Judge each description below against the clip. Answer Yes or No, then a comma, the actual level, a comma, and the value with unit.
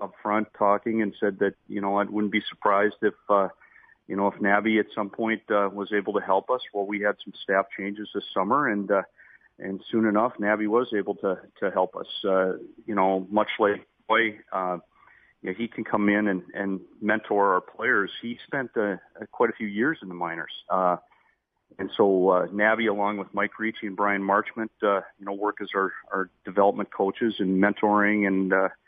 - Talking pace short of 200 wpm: No, fast, 205 wpm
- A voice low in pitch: Yes, low, 100 Hz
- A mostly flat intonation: Yes, narrow, 1.4 semitones